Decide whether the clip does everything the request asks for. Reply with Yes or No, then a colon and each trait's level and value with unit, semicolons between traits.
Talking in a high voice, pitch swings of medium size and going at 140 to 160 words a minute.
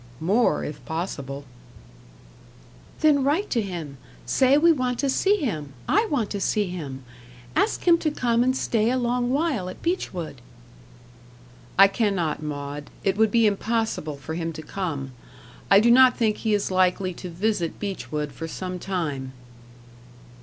No: high, 195 Hz; wide, 7.5 semitones; average, 155 wpm